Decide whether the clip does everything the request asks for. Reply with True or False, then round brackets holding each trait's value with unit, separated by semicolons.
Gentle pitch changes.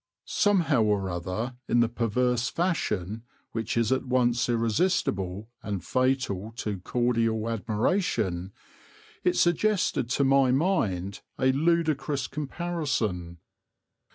False (4.9 semitones)